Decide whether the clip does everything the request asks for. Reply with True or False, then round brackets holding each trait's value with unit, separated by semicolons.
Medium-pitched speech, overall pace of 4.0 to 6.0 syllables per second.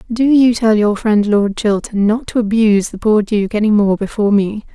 False (215 Hz; 5.1 syllables/s)